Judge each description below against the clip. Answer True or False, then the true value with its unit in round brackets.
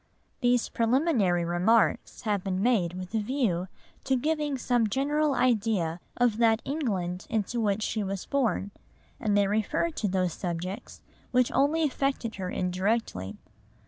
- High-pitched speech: True (220 Hz)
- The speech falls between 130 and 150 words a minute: True (145 wpm)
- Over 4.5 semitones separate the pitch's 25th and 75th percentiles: True (5.2 semitones)